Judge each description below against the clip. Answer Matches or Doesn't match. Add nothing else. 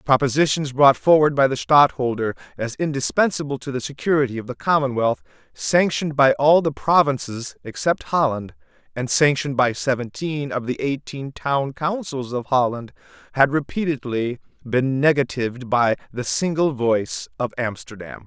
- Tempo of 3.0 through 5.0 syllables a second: Matches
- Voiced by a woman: Doesn't match